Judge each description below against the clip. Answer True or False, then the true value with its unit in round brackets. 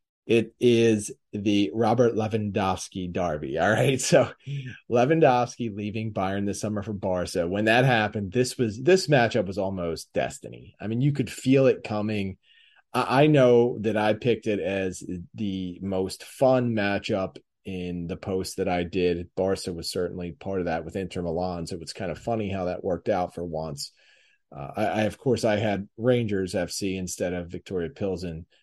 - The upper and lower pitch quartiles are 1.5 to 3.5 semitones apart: False (4.1 semitones)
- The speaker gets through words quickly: False (180 wpm)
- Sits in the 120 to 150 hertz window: False (100 Hz)